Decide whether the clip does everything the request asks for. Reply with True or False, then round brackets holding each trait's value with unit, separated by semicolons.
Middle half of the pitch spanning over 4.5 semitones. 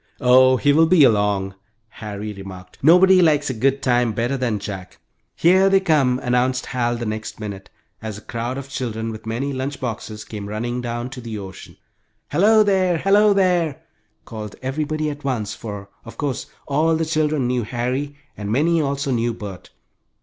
True (5.4 semitones)